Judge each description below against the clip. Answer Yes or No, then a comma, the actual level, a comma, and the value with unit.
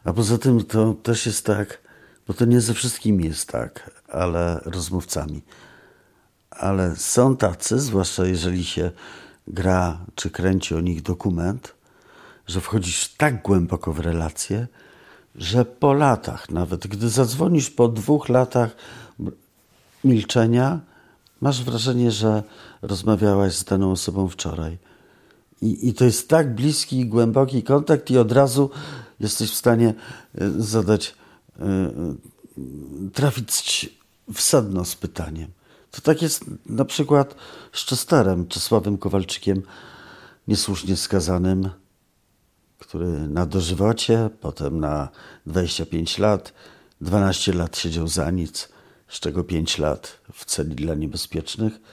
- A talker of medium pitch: No, low, 100 Hz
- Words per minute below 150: Yes, average, 120 wpm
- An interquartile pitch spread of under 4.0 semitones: No, average, 5.1 semitones